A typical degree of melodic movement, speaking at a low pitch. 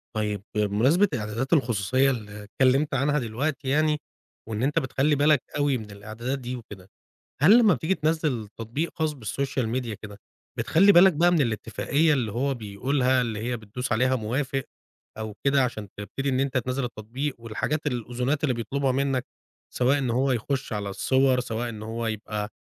Yes: average, 4.1 semitones; low, 125 Hz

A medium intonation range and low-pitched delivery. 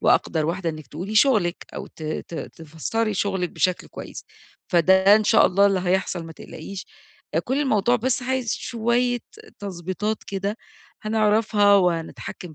No: average, 4.0 semitones; high, 195 Hz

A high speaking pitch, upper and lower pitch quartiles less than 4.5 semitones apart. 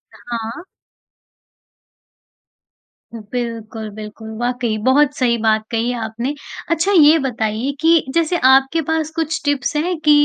No: very high, 250 Hz; average, 5.3 semitones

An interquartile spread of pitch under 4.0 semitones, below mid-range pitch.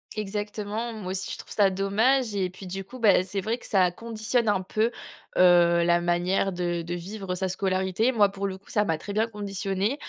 No: average, 2.7 semitones; high, 195 Hz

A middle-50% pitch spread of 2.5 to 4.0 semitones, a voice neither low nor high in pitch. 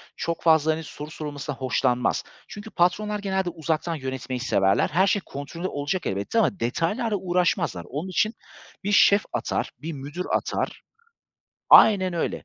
No: average, 5.0 semitones; medium, 165 Hz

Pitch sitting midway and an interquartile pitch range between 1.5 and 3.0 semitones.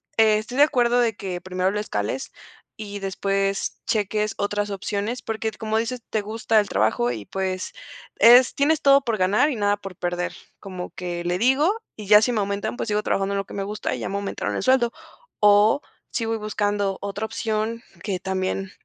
No: high, 205 Hz; narrow, 2.6 semitones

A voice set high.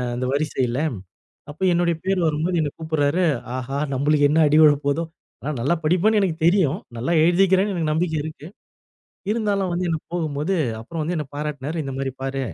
No: medium, 155 Hz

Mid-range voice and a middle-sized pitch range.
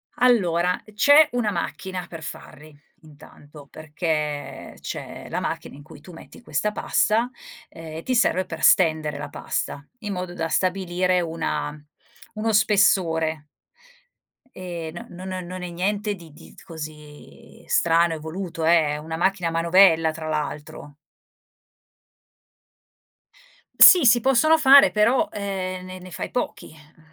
Yes: medium, 175 Hz; average, 3.9 semitones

